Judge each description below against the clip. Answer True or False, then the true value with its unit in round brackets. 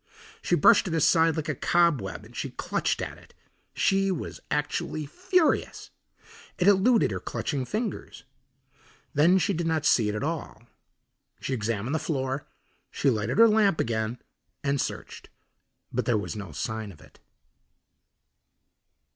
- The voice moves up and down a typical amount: False (7.2 semitones)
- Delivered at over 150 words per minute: False (145 wpm)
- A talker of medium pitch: True (150 Hz)